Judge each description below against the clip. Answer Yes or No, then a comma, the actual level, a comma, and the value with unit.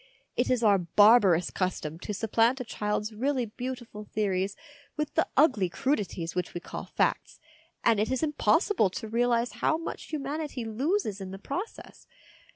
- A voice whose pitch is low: No, high, 225 Hz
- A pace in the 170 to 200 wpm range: No, average, 160 wpm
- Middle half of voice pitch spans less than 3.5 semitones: No, average, 4.8 semitones